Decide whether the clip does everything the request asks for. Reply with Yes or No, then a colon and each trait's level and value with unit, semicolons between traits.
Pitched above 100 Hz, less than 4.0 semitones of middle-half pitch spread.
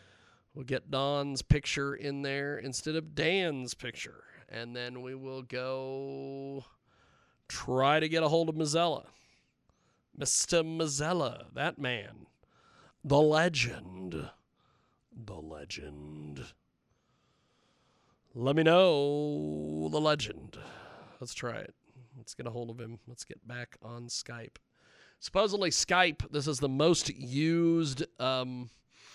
No: low, 135 Hz; average, 4.4 semitones